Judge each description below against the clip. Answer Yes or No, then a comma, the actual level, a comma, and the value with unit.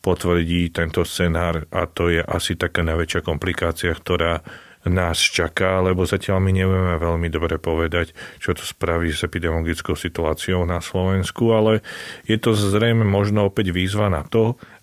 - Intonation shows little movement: Yes, narrow, 2.2 semitones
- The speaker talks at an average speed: Yes, average, 150 wpm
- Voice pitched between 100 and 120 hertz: No, very low, 90 Hz